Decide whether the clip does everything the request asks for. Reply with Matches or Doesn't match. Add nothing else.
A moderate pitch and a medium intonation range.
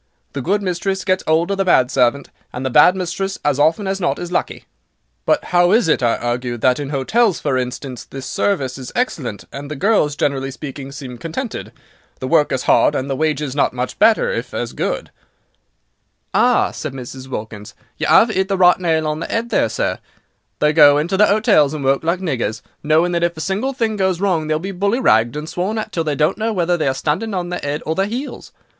Doesn't match